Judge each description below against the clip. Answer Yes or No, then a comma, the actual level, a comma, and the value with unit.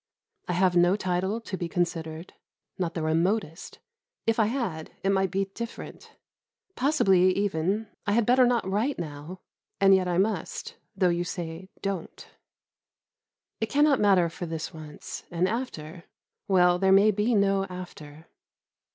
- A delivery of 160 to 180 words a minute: No, average, 150 wpm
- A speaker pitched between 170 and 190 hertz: Yes, medium, 185 Hz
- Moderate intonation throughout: Yes, average, 3.2 semitones